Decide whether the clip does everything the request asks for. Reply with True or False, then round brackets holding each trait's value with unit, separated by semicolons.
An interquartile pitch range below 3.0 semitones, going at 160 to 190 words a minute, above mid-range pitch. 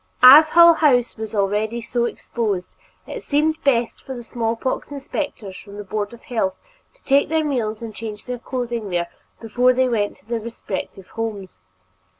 False (3.6 semitones; 175 wpm; 235 Hz)